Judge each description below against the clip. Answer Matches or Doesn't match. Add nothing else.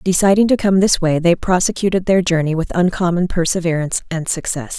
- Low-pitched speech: Doesn't match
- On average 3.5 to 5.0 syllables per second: Doesn't match